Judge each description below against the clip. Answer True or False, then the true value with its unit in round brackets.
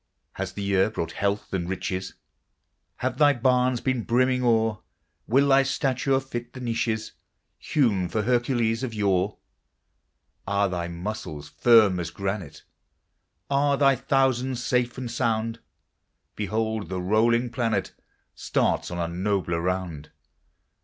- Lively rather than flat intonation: False (4.7 semitones)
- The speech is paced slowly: True (130 wpm)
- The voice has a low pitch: True (110 Hz)